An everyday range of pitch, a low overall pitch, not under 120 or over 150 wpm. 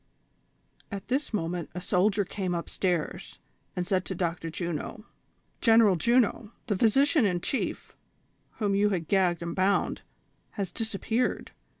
No: average, 3.7 semitones; high, 195 Hz; slow, 135 wpm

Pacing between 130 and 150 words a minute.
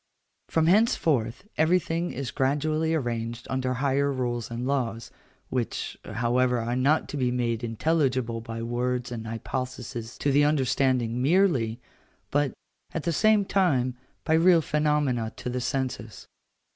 Yes: slow, 135 wpm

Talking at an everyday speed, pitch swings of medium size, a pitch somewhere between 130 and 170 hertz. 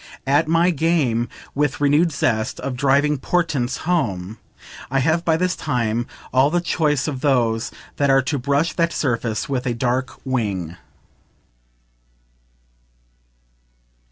No: slow, 125 wpm; average, 4.6 semitones; low, 135 Hz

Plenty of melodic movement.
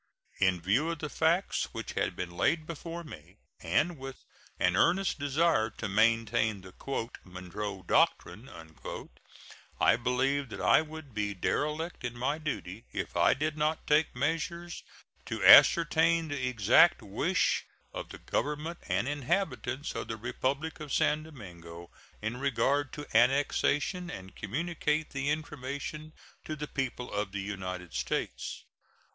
Yes: wide, 6.7 semitones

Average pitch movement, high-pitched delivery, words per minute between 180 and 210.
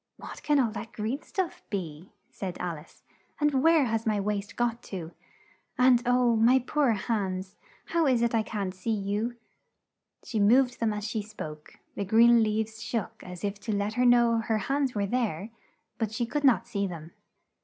Yes: average, 3.4 semitones; high, 220 Hz; average, 185 wpm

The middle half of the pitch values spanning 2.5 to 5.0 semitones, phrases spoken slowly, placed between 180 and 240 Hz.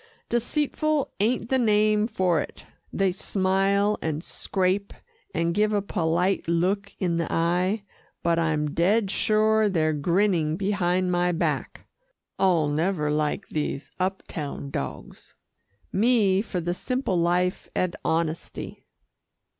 Yes: average, 3.7 semitones; slow, 125 wpm; medium, 185 Hz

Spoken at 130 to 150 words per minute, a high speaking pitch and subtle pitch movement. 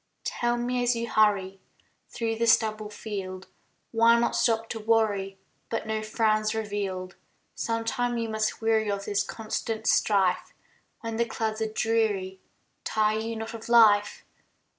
Yes: average, 145 wpm; high, 220 Hz; narrow, 1.7 semitones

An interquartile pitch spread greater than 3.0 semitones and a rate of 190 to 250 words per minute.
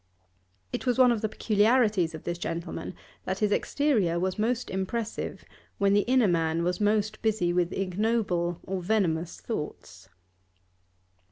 No: average, 4.2 semitones; average, 145 wpm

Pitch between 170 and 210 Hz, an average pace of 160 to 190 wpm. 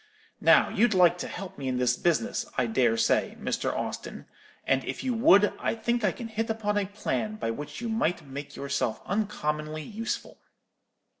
Yes: medium, 185 Hz; average, 180 wpm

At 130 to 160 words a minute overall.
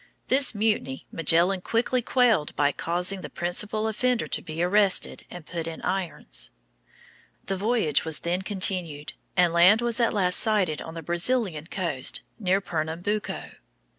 Yes: average, 145 wpm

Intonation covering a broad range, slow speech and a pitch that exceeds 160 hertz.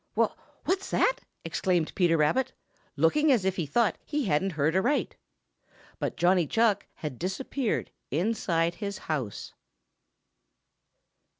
Yes: wide, 6.1 semitones; slow, 120 wpm; high, 190 Hz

